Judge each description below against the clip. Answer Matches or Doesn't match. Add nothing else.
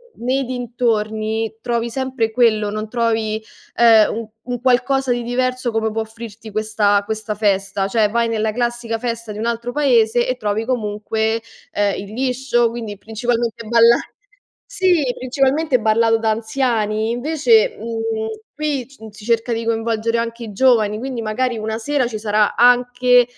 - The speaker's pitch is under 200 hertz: Doesn't match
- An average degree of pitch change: Doesn't match